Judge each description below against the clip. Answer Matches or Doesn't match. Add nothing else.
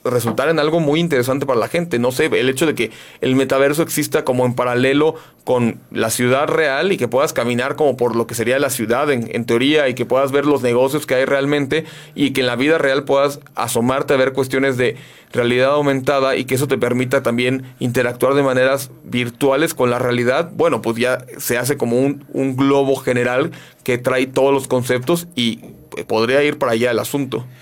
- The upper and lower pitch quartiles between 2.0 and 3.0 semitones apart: Matches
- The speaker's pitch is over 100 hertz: Matches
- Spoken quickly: Matches